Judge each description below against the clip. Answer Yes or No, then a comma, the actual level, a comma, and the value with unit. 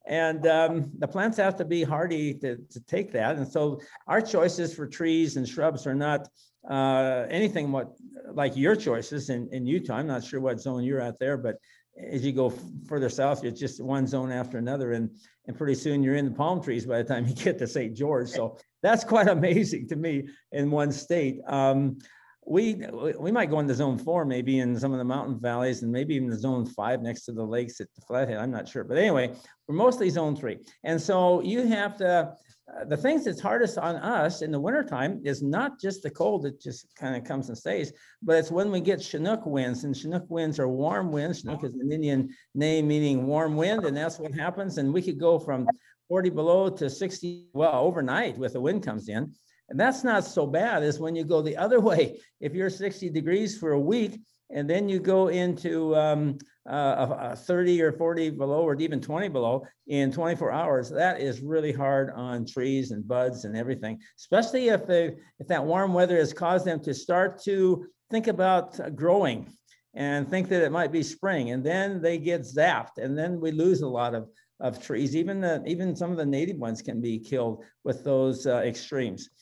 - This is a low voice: No, medium, 150 Hz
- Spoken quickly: Yes, fast, 215 wpm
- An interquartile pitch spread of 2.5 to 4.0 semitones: No, average, 4.9 semitones